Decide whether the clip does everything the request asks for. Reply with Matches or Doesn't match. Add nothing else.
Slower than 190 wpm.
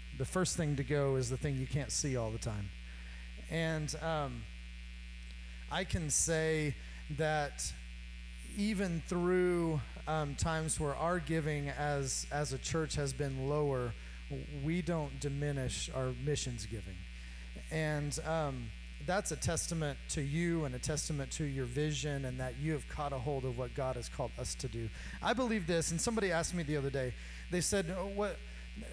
Matches